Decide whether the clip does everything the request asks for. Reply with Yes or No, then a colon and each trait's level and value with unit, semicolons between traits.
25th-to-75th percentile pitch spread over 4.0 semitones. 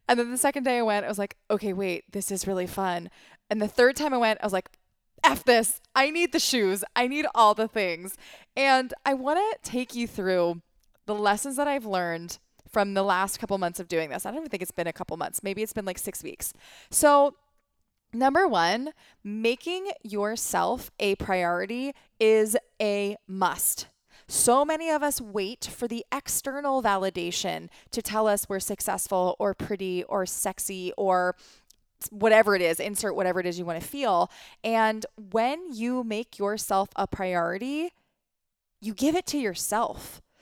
Yes: average, 4.8 semitones